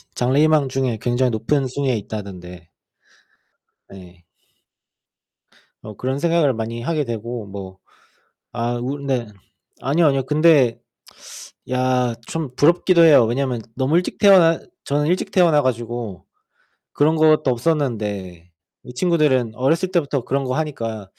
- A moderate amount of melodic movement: Yes, average, 4.8 semitones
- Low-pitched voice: Yes, low, 130 Hz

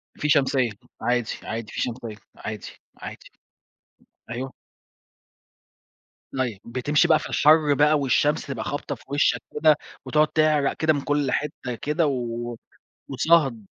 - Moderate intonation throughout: Yes, average, 3.7 semitones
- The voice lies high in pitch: No, medium, 140 Hz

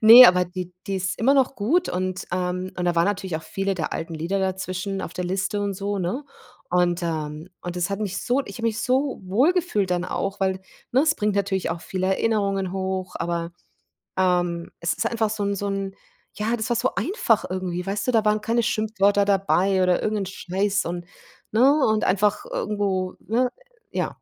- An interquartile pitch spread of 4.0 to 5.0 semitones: No, average, 2.9 semitones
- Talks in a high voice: Yes, high, 195 Hz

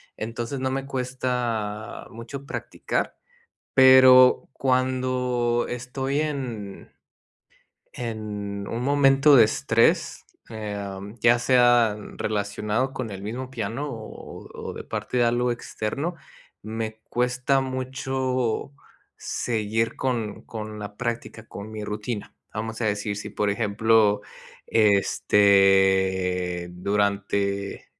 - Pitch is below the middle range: Yes, low, 115 Hz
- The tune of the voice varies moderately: Yes, average, 3.7 semitones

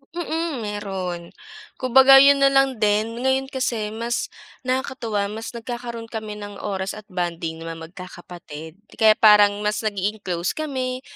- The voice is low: No, high, 215 Hz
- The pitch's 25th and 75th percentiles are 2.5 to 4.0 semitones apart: No, average, 4.7 semitones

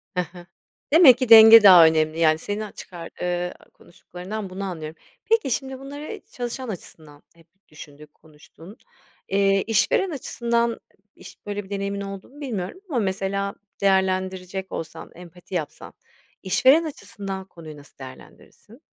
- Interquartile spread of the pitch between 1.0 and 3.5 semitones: No, average, 4.8 semitones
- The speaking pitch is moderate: No, high, 195 Hz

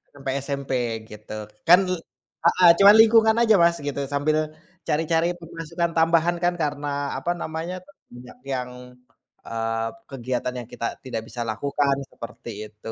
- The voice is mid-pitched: Yes, medium, 145 Hz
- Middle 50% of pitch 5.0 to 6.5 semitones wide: Yes, average, 5.3 semitones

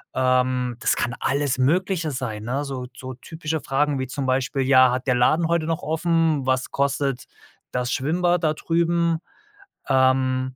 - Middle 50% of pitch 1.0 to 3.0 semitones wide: No, average, 3.8 semitones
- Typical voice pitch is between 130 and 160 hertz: Yes, low, 135 Hz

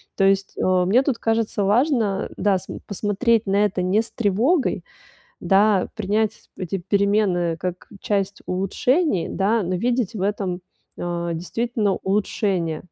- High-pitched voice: Yes, high, 200 Hz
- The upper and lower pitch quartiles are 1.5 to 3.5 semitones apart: Yes, average, 3.0 semitones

